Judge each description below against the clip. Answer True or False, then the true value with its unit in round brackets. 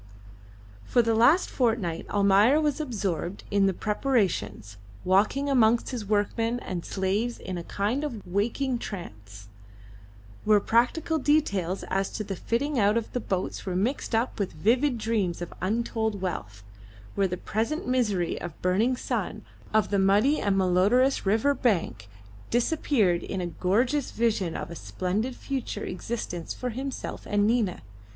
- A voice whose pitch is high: True (210 Hz)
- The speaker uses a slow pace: False (150 wpm)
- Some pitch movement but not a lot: True (4.6 semitones)